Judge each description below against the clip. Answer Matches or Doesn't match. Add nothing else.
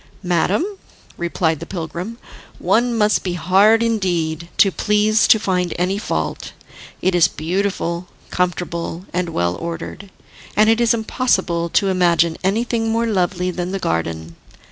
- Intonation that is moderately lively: Matches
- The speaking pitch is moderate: Matches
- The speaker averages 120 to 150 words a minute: Matches